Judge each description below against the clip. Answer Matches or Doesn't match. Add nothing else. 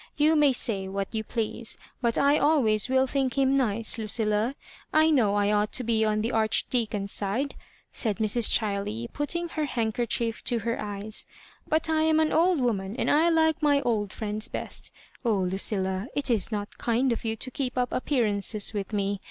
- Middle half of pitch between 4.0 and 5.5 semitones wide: Matches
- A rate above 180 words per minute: Matches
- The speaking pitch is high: Matches